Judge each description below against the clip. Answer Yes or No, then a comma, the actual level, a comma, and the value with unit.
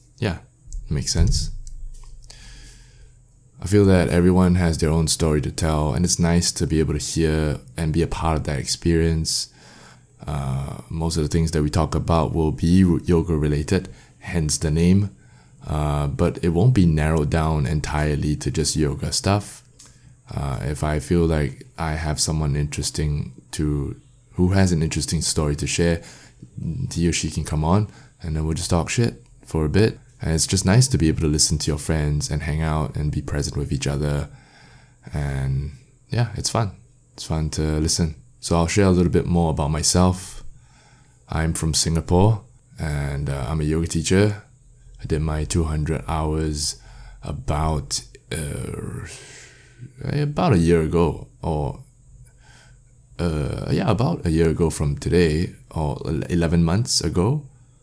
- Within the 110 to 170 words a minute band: Yes, average, 165 wpm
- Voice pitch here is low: Yes, very low, 80 Hz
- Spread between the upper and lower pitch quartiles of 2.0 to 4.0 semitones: No, average, 5.0 semitones